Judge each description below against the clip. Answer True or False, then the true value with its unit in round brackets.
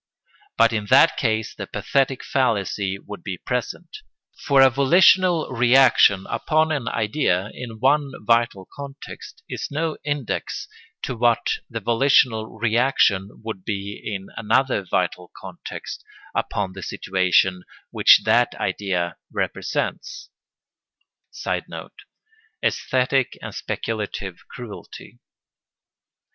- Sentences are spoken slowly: True (105 wpm)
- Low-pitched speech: True (115 Hz)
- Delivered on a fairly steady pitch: False (5.2 semitones)